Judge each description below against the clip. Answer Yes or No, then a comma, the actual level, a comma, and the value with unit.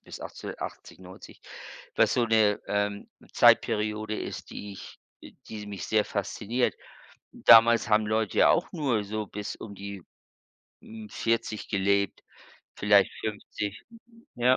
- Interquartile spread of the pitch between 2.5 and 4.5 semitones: No, narrow, 1.6 semitones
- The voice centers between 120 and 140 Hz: No, low, 105 Hz